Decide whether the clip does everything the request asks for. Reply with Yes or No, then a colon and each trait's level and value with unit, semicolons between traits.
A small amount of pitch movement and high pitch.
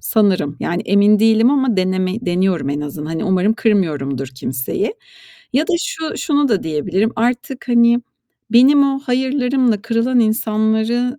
No: average, 5.2 semitones; high, 220 Hz